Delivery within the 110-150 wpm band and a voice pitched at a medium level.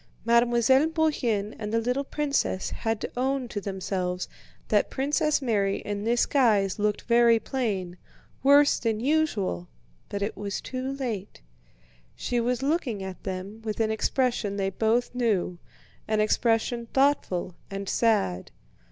No: average, 140 wpm; high, 225 Hz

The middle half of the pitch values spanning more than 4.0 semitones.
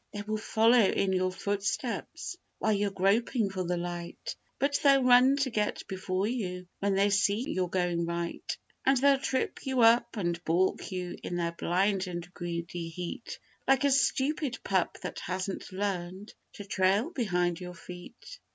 Yes: average, 4.8 semitones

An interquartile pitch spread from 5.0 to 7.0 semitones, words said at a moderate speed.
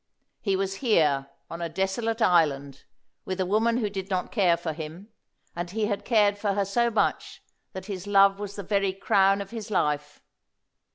No: average, 3.0 semitones; average, 185 wpm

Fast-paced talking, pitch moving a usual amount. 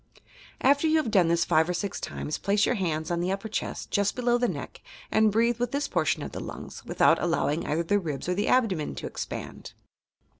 No: fast, 220 wpm; wide, 5.8 semitones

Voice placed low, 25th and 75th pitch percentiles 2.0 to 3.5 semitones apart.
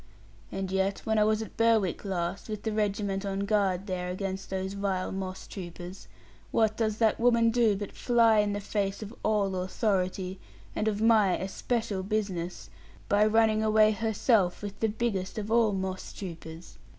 No: high, 205 Hz; narrow, 2.4 semitones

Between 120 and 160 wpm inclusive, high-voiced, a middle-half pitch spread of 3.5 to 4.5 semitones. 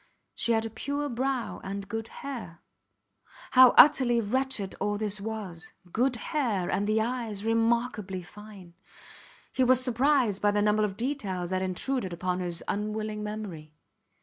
Yes: average, 150 wpm; high, 215 Hz; average, 4.0 semitones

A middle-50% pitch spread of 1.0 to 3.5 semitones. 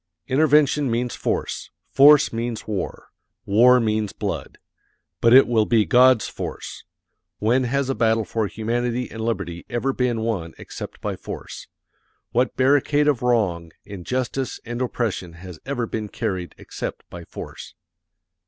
Yes: average, 3.1 semitones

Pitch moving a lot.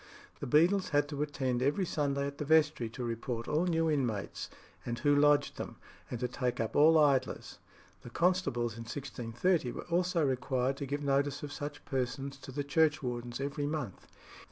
No: average, 3.2 semitones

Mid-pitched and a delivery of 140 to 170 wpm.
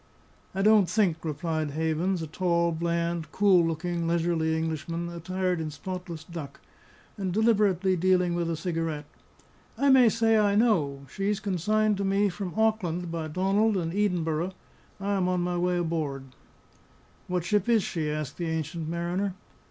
Yes: medium, 175 Hz; average, 155 wpm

